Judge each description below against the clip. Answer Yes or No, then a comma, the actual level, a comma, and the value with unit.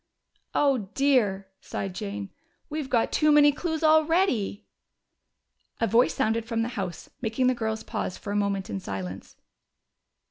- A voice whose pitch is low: No, high, 225 Hz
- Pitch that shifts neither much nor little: No, wide, 5.9 semitones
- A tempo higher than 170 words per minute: No, average, 145 wpm